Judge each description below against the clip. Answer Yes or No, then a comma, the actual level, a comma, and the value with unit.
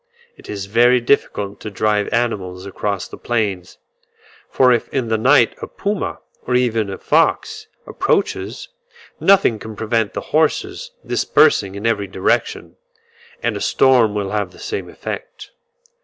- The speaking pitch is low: Yes, low, 110 Hz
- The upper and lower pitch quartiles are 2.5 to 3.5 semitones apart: No, average, 4.3 semitones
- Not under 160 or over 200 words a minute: No, average, 145 wpm